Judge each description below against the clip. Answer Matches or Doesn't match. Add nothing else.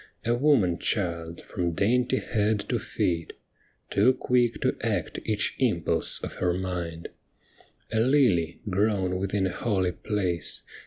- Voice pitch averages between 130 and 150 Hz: Doesn't match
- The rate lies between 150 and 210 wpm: Doesn't match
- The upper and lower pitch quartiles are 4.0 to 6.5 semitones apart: Matches